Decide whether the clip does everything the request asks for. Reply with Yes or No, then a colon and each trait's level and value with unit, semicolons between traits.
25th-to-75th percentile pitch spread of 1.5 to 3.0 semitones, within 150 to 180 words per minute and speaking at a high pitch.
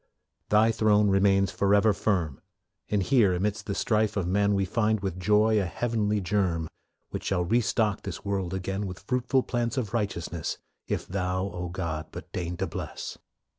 No: narrow, 2.6 semitones; average, 170 wpm; low, 100 Hz